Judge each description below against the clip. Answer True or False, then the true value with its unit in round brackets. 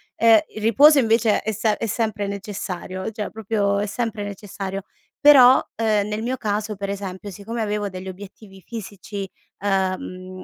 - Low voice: False (205 Hz)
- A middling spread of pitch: False (2.1 semitones)